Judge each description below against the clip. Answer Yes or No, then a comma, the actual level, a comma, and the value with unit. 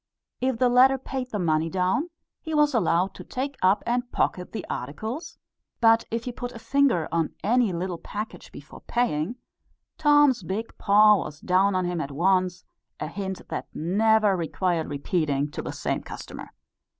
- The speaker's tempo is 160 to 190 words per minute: Yes, average, 170 wpm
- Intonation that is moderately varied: No, wide, 5.7 semitones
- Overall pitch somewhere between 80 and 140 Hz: No, high, 200 Hz